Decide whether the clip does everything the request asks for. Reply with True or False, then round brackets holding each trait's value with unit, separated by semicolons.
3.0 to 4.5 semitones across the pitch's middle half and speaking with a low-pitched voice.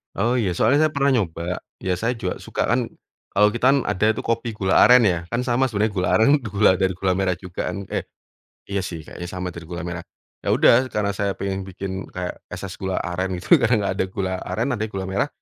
True (4.0 semitones; 100 Hz)